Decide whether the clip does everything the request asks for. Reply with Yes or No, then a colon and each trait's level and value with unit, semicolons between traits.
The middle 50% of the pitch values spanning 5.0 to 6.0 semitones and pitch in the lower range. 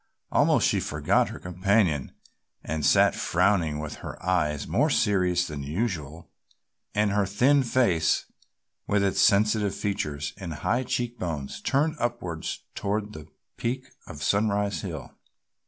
Yes: average, 5.3 semitones; low, 100 Hz